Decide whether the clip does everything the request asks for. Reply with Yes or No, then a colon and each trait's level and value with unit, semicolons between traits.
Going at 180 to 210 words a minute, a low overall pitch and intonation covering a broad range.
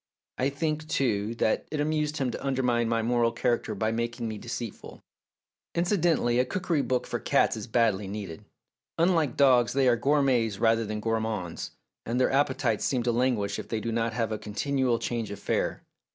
No: average, 185 wpm; low, 120 Hz; average, 3.5 semitones